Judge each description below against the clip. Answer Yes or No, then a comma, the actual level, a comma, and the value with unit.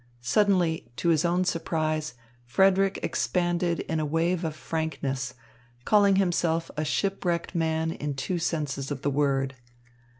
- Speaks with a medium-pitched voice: Yes, medium, 160 Hz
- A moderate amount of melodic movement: Yes, average, 3.3 semitones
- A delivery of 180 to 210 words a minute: No, slow, 135 wpm